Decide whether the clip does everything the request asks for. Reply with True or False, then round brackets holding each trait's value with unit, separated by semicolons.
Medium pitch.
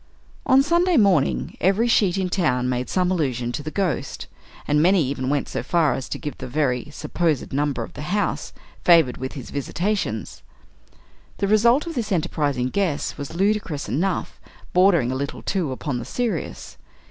True (160 Hz)